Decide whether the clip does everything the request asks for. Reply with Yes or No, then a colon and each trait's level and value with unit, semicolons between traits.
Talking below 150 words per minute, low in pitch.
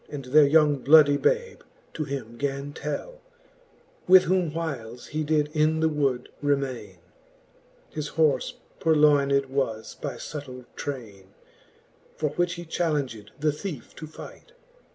No: slow, 135 wpm; medium, 145 Hz